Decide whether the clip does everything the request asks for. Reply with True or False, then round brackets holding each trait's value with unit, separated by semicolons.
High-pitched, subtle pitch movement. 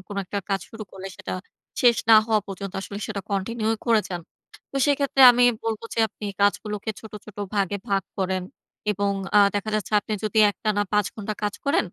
True (210 Hz; 1.9 semitones)